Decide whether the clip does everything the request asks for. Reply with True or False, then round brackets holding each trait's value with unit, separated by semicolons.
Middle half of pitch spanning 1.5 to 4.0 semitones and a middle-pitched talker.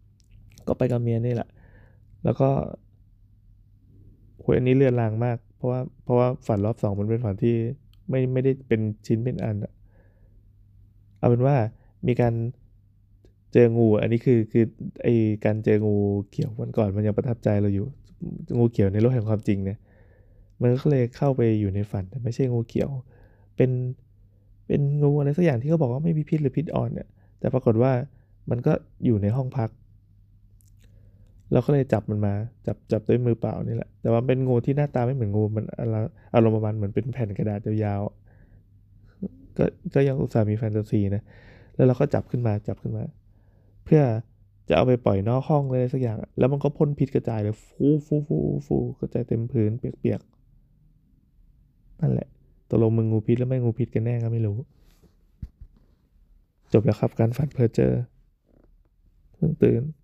False (3.4 semitones; 110 Hz)